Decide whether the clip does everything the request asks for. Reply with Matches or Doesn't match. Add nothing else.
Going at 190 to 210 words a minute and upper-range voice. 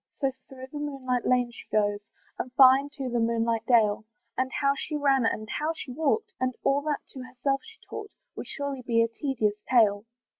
Matches